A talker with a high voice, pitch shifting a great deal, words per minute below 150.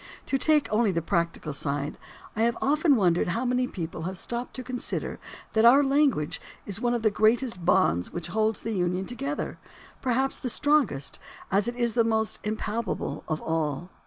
No: high, 220 Hz; wide, 6.1 semitones; average, 180 wpm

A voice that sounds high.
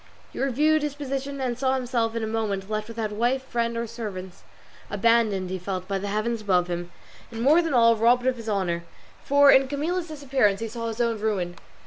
Yes: high, 230 Hz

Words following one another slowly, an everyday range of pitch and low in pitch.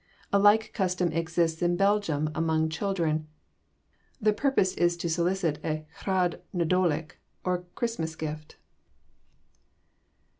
No: slow, 110 wpm; average, 3.1 semitones; medium, 175 Hz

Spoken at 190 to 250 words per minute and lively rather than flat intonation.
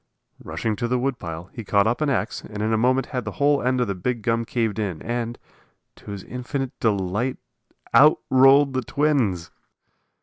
No: average, 195 wpm; average, 3.7 semitones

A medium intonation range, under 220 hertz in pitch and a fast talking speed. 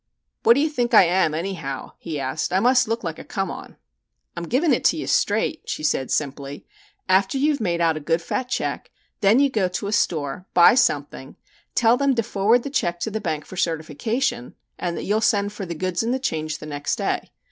No: wide, 6.9 semitones; high, 190 Hz; fast, 225 wpm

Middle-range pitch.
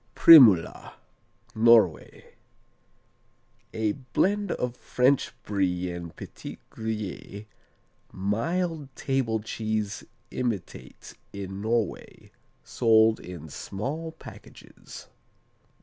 No: low, 110 Hz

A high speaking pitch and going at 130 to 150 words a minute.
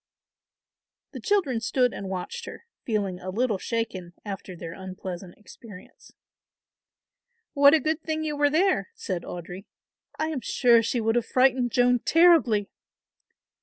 Yes: high, 235 Hz; average, 140 wpm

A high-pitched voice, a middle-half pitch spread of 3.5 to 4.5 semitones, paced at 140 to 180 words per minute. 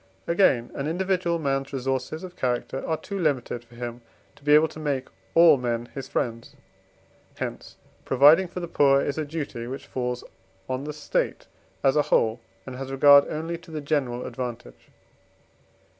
No: medium, 140 Hz; average, 3.9 semitones; average, 170 wpm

